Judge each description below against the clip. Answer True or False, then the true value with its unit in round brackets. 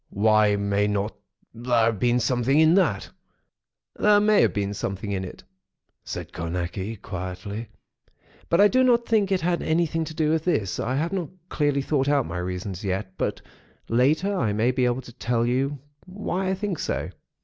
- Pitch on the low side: True (125 Hz)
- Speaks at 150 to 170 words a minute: False (180 wpm)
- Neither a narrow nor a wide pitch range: False (8.2 semitones)